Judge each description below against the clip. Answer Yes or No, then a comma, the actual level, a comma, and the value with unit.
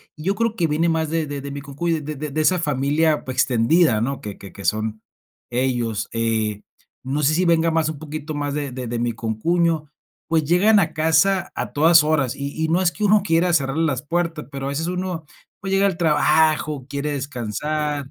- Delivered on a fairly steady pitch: No, average, 3.6 semitones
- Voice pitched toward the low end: No, medium, 150 Hz